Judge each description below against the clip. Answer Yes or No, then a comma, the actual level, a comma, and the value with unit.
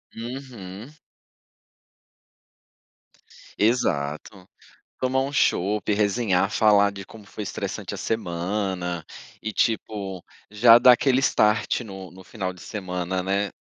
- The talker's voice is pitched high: No, low, 100 Hz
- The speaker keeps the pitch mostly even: No, average, 3.3 semitones